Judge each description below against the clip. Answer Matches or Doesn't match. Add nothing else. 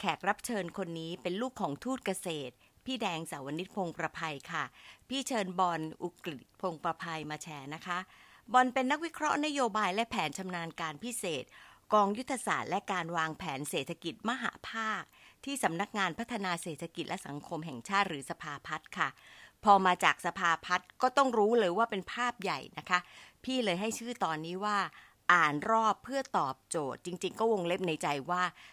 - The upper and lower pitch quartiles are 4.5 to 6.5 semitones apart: Matches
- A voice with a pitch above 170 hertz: Matches